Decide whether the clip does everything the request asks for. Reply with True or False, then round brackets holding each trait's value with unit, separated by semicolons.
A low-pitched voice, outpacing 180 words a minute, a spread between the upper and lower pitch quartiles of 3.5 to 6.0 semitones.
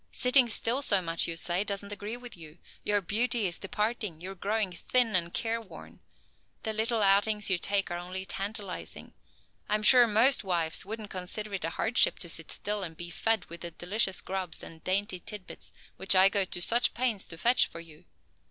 False (200 Hz; 200 wpm; 3.9 semitones)